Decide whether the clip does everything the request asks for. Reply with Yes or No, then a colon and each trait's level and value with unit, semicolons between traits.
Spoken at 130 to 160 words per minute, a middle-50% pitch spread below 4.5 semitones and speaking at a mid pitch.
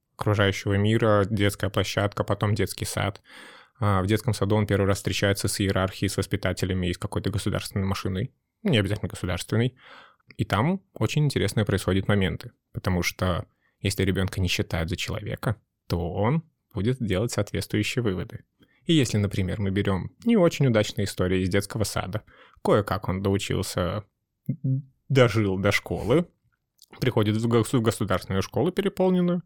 No: average, 140 wpm; average, 3.2 semitones; low, 105 Hz